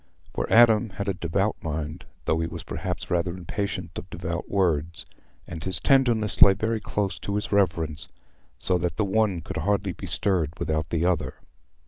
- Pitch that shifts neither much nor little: Yes, average, 3.6 semitones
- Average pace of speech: Yes, average, 175 wpm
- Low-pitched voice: Yes, very low, 95 Hz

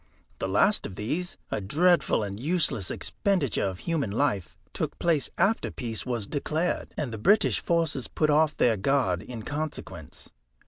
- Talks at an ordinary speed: Yes, average, 155 wpm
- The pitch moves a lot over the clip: Yes, wide, 7.8 semitones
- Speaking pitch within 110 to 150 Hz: Yes, medium, 140 Hz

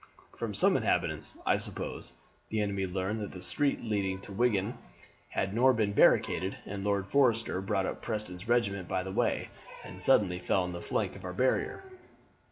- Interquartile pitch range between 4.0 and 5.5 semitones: No, average, 2.8 semitones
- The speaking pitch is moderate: No, low, 100 Hz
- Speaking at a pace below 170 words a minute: No, average, 175 wpm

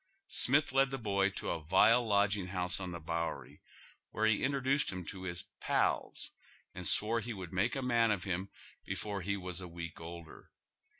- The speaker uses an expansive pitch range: No, average, 4.3 semitones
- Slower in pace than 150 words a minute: No, average, 195 wpm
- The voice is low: Yes, low, 100 Hz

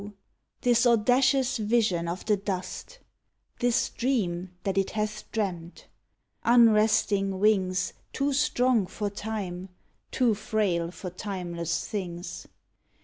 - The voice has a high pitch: Yes, high, 210 Hz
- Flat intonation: No, average, 4.0 semitones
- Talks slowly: Yes, slow, 110 wpm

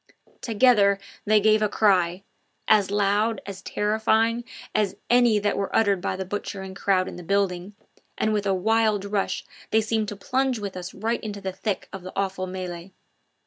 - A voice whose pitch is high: Yes, high, 205 Hz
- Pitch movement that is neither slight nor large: No, narrow, 2.3 semitones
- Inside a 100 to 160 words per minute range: No, average, 180 wpm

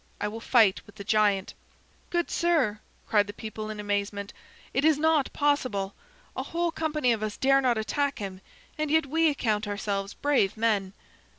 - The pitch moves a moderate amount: No, wide, 6.1 semitones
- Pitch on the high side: Yes, high, 220 Hz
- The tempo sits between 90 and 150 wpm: No, average, 175 wpm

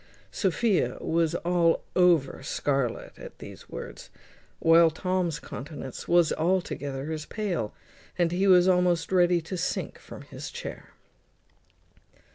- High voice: No, medium, 170 Hz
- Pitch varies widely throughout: No, narrow, 2.4 semitones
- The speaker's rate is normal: No, slow, 120 wpm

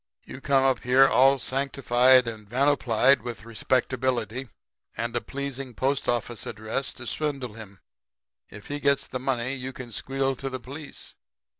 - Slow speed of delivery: No, average, 155 wpm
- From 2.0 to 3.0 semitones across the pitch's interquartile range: Yes, narrow, 2.4 semitones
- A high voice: No, low, 130 Hz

